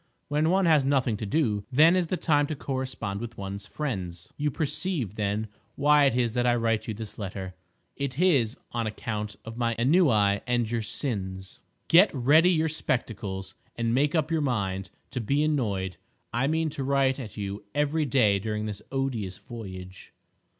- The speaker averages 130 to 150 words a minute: No, average, 175 wpm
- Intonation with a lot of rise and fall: Yes, wide, 6.0 semitones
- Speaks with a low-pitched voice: Yes, low, 120 Hz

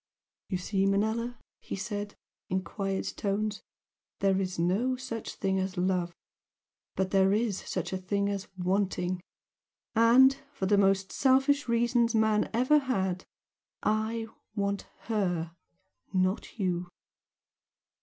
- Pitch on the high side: Yes, high, 200 Hz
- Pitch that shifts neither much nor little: Yes, average, 3.4 semitones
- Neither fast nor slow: No, slow, 125 wpm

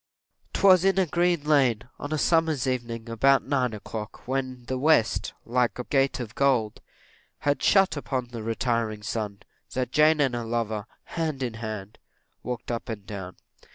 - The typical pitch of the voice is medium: No, low, 125 Hz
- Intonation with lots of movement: No, average, 4.2 semitones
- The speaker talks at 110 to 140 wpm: No, average, 165 wpm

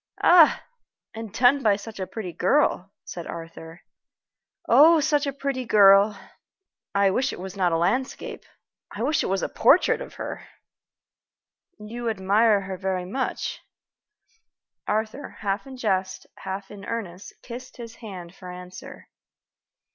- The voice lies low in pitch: No, high, 205 Hz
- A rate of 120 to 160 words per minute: Yes, average, 140 wpm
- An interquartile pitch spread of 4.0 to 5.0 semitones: Yes, average, 4.6 semitones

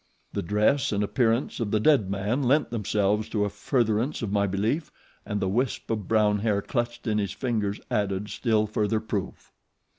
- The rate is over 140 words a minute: Yes, average, 180 wpm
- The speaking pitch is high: No, low, 105 Hz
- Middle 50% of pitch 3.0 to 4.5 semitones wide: No, narrow, 2.5 semitones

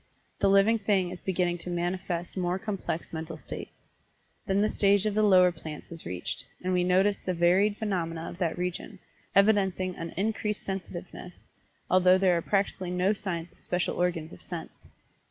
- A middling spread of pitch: No, narrow, 2.1 semitones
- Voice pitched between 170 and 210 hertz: Yes, medium, 185 Hz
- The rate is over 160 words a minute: Yes, average, 170 wpm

